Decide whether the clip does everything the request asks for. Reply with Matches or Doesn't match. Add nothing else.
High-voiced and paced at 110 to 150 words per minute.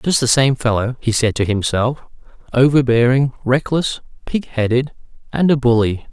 Doesn't match